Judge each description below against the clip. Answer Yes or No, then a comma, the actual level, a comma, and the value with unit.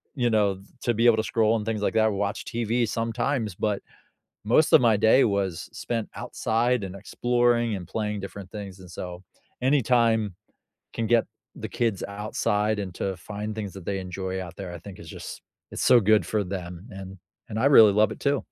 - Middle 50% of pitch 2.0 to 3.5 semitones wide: Yes, average, 2.9 semitones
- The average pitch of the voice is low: Yes, low, 105 Hz